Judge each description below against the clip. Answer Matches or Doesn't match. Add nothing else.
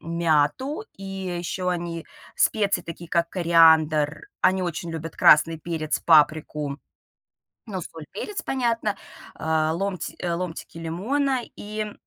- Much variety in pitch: Doesn't match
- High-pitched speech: Doesn't match